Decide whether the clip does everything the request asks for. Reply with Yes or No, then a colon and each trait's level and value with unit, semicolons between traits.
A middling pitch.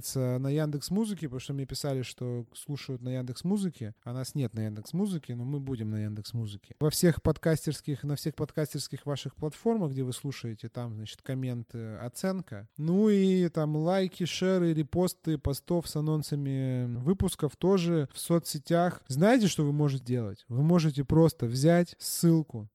Yes: medium, 145 Hz